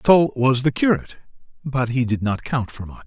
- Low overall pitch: Yes, low, 130 Hz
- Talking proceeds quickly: Yes, fast, 215 wpm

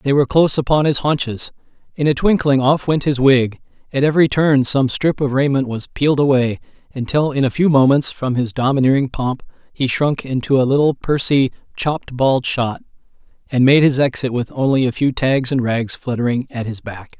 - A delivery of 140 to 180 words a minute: No, average, 195 wpm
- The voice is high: No, low, 135 Hz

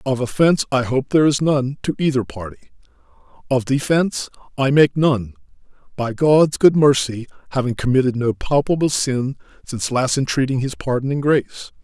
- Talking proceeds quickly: No, average, 145 wpm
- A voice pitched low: Yes, low, 130 Hz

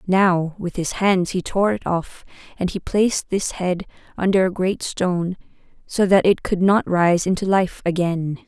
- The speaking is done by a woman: Yes, female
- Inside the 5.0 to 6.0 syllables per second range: No, 4.4 syllables/s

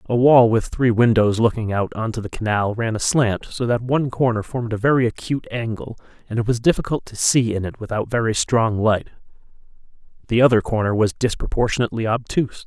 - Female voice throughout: No, male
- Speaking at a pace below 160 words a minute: No, average, 190 wpm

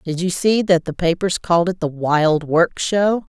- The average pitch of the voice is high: No, medium, 175 Hz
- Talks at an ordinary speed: No, fast, 215 wpm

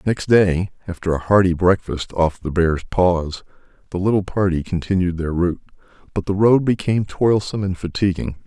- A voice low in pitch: Yes, very low, 90 Hz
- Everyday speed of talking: Yes, average, 165 wpm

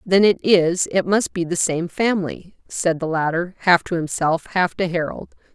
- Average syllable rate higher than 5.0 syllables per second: No, 4.7 syllables/s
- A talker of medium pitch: Yes, medium, 175 Hz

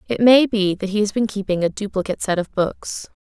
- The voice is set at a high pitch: Yes, high, 205 Hz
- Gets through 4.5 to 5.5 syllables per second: No, 5.7 syllables/s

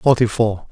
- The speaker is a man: Yes, male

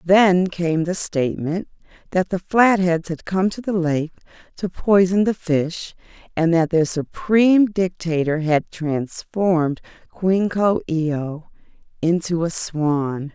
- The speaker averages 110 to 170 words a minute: Yes, slow, 135 wpm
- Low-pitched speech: No, medium, 175 Hz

